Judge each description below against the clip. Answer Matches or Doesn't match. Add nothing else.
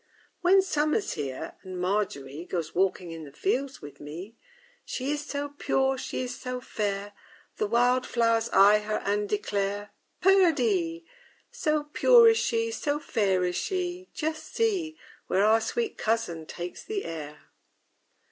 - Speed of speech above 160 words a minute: Doesn't match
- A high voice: Matches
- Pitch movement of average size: Doesn't match